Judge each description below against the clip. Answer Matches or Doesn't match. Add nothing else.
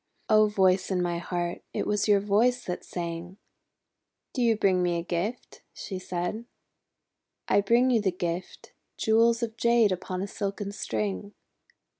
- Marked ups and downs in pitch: Doesn't match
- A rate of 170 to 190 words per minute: Doesn't match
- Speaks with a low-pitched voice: Doesn't match